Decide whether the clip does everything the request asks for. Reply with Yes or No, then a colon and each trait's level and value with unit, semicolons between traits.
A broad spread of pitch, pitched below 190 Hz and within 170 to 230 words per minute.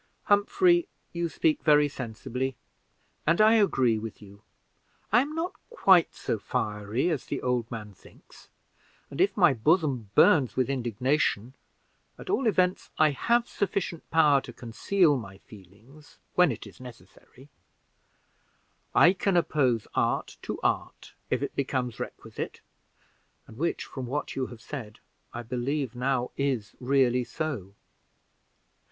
No: wide, 6.5 semitones; low, 135 Hz; slow, 135 wpm